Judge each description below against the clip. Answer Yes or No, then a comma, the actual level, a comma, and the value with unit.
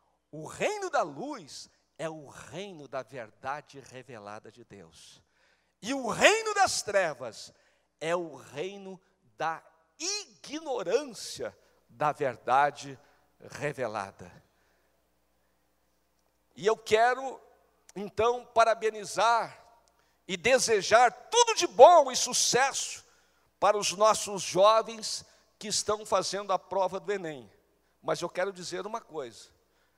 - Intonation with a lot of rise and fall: Yes, wide, 8.2 semitones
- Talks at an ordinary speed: No, slow, 110 wpm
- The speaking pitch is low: No, high, 200 Hz